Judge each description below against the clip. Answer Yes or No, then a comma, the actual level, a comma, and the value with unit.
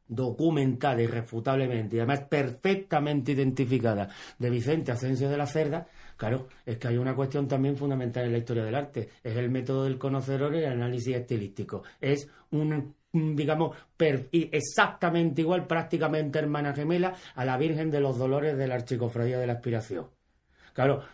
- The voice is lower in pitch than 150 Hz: Yes, low, 135 Hz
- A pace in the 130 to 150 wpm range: No, average, 160 wpm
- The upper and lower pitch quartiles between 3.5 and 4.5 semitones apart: Yes, average, 3.8 semitones